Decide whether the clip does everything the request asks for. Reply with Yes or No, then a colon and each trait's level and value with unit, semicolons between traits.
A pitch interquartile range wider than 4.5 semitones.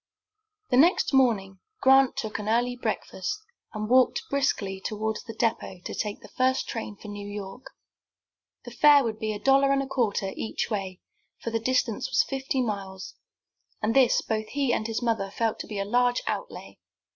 No: average, 3.7 semitones